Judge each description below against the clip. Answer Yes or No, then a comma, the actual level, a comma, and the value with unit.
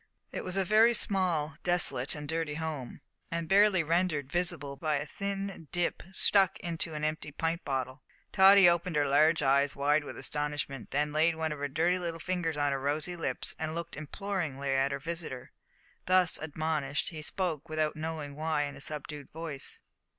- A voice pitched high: No, medium, 155 Hz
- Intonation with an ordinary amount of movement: Yes, average, 3.2 semitones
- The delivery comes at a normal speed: Yes, average, 180 wpm